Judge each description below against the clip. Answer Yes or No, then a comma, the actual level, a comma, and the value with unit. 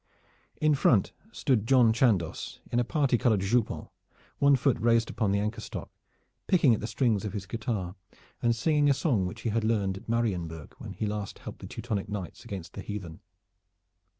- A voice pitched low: Yes, low, 110 Hz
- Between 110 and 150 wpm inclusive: No, average, 185 wpm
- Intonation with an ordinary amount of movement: Yes, average, 3.6 semitones